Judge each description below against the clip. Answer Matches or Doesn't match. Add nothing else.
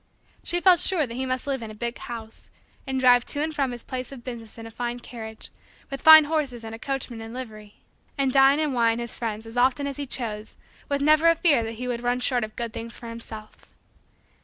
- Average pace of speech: Doesn't match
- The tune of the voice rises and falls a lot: Doesn't match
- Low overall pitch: Doesn't match